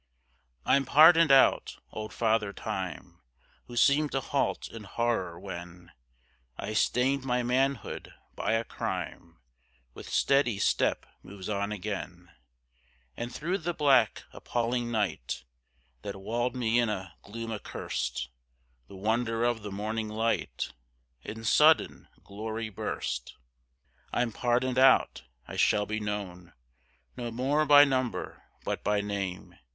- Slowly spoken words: Yes, slow, 125 wpm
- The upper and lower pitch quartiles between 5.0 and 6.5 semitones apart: No, average, 3.8 semitones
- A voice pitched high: No, low, 115 Hz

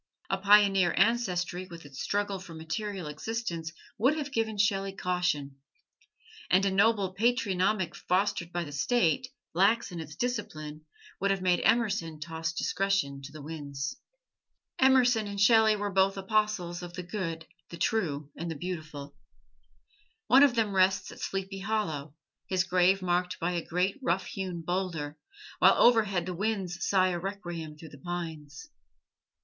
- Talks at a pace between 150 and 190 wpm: Yes, average, 155 wpm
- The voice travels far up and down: No, average, 3.7 semitones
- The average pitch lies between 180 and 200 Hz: Yes, medium, 185 Hz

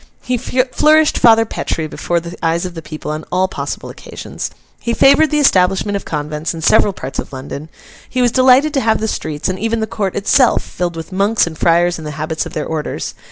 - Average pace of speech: No, fast, 215 wpm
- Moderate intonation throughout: No, wide, 6.5 semitones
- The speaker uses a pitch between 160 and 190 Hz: Yes, medium, 185 Hz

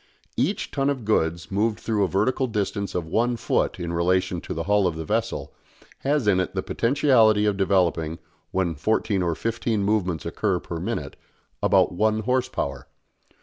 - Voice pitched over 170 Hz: No, low, 100 Hz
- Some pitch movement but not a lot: Yes, average, 4.5 semitones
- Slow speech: No, average, 175 wpm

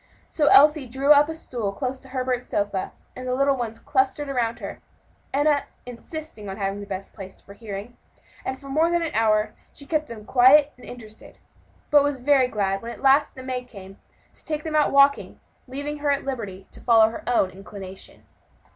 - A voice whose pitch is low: No, very high, 255 Hz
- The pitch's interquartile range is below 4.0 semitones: No, average, 5.0 semitones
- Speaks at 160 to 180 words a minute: No, average, 200 wpm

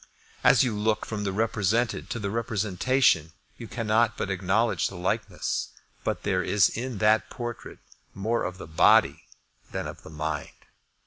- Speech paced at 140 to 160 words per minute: Yes, average, 155 wpm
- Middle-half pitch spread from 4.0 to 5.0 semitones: No, average, 3.5 semitones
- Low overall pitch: Yes, low, 105 Hz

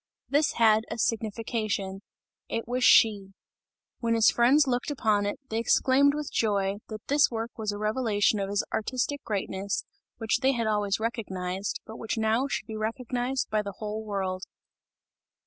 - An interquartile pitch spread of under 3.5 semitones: Yes, average, 3.0 semitones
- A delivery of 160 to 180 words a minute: Yes, average, 165 wpm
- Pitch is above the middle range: Yes, high, 220 Hz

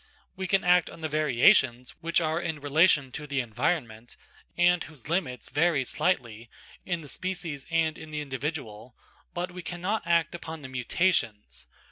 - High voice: No, medium, 155 Hz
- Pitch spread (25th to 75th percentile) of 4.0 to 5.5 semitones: Yes, average, 5.2 semitones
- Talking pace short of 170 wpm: Yes, average, 160 wpm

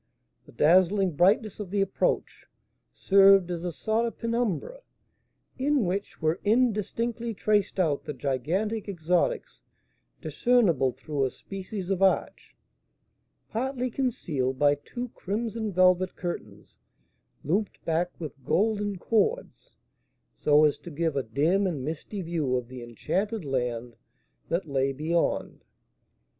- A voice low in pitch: No, medium, 185 Hz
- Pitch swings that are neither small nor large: No, wide, 6.2 semitones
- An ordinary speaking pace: No, slow, 125 wpm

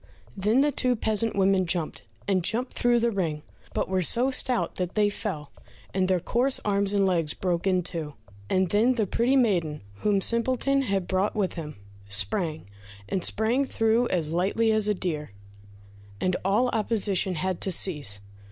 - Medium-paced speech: Yes, average, 170 wpm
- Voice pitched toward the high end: Yes, high, 195 Hz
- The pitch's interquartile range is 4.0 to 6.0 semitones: Yes, average, 4.3 semitones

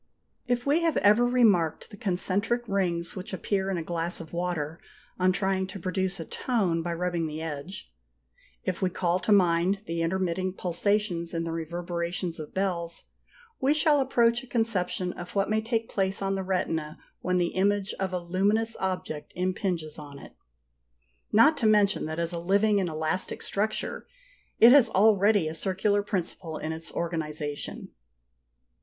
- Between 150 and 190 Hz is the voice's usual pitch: Yes, medium, 185 Hz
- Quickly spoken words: No, average, 165 wpm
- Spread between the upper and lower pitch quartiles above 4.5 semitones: No, average, 3.3 semitones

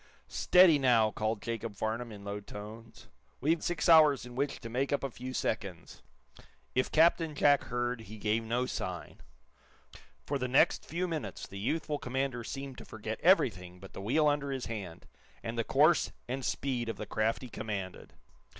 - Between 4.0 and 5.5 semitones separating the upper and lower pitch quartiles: Yes, average, 4.4 semitones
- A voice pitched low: Yes, low, 120 Hz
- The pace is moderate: Yes, average, 175 wpm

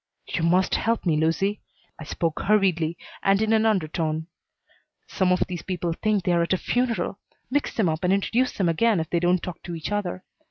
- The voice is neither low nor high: Yes, medium, 180 Hz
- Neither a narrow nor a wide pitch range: Yes, average, 3.8 semitones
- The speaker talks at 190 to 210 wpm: Yes, average, 200 wpm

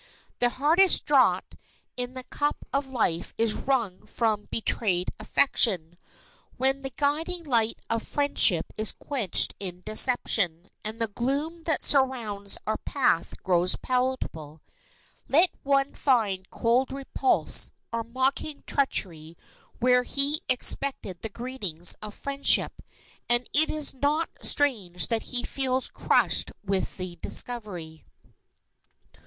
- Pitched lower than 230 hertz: No, high, 245 Hz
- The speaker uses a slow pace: Yes, slow, 120 wpm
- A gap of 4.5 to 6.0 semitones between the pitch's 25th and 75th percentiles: Yes, wide, 5.4 semitones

